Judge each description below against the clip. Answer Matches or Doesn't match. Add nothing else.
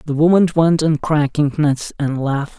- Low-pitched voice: Doesn't match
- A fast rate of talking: Doesn't match